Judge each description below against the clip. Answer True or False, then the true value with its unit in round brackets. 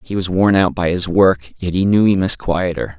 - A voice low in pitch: True (90 Hz)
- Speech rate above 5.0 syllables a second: False (4.9 syllables/s)